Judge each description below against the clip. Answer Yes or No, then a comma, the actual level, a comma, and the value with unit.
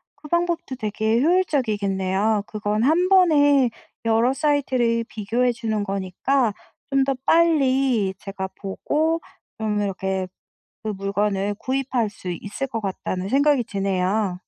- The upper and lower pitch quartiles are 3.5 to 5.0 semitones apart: No, wide, 5.4 semitones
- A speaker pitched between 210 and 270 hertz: Yes, high, 225 Hz